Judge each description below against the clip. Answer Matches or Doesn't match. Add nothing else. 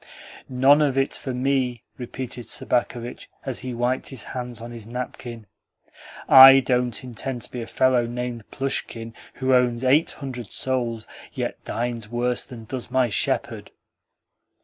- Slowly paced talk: Doesn't match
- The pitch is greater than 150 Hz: Doesn't match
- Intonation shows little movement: Matches